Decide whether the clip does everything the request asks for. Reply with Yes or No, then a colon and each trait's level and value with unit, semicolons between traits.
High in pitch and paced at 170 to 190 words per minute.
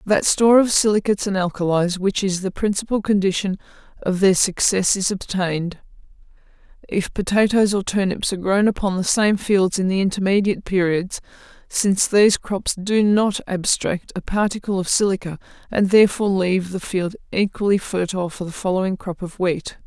No: high, 195 Hz; average, 160 wpm